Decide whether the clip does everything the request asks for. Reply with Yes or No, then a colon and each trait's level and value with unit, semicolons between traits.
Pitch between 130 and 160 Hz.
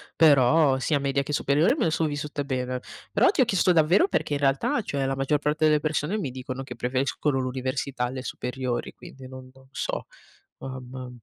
Yes: low, 135 Hz